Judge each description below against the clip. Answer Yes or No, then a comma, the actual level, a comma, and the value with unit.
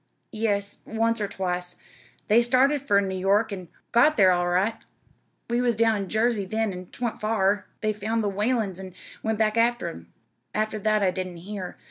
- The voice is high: Yes, high, 210 Hz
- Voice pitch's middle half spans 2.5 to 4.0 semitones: Yes, average, 2.9 semitones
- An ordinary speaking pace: Yes, average, 185 wpm